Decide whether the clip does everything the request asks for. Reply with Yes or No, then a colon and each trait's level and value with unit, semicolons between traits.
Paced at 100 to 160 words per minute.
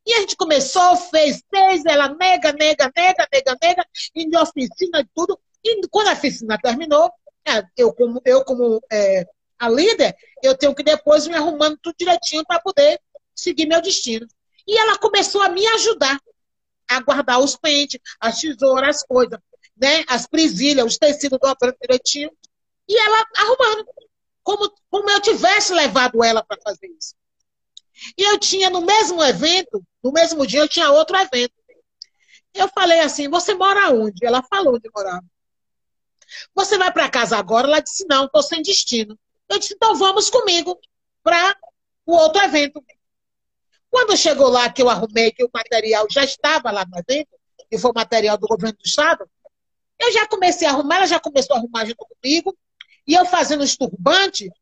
No: average, 170 wpm